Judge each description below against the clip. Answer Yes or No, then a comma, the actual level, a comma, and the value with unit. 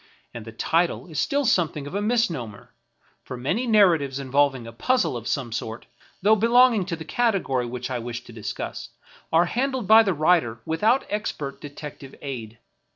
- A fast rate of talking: No, average, 175 wpm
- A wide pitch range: Yes, wide, 9.0 semitones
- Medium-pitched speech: Yes, medium, 155 Hz